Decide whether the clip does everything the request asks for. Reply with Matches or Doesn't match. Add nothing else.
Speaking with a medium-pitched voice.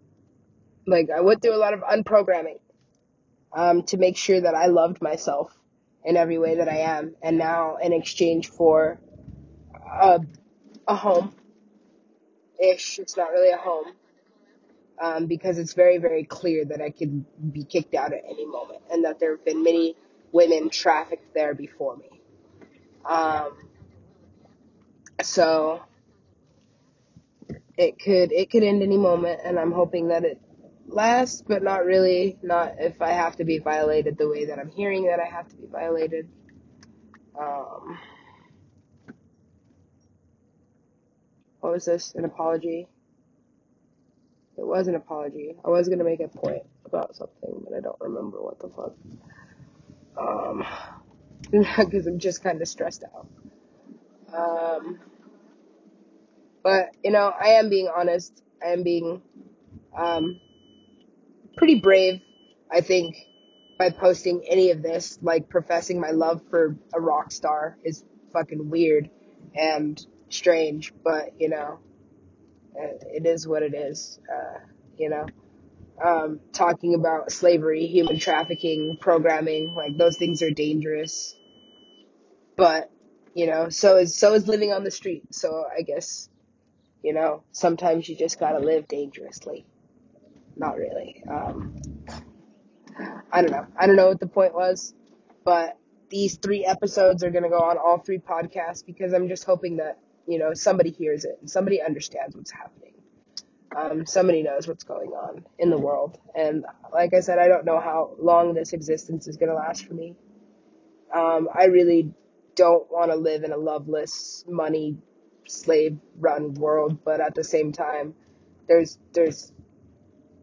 Matches